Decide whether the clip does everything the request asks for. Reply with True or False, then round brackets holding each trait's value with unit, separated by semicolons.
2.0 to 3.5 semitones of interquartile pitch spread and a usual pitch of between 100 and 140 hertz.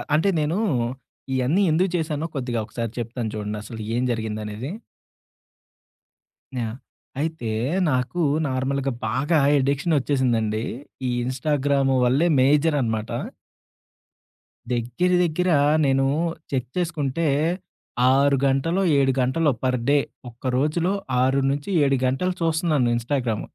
False (4.0 semitones; 135 Hz)